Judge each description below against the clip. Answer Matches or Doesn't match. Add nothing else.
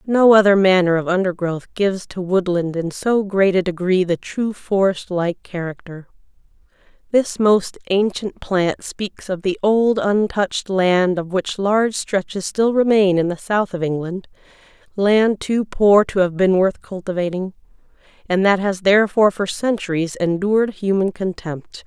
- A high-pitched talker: Matches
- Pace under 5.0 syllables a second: Matches